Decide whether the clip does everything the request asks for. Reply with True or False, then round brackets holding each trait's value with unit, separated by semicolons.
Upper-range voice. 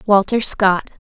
True (200 Hz)